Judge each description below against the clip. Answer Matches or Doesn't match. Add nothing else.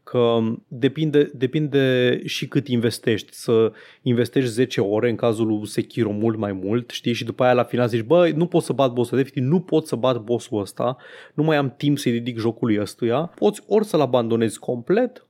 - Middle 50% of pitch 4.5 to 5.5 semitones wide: Doesn't match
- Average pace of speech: Doesn't match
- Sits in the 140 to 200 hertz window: Doesn't match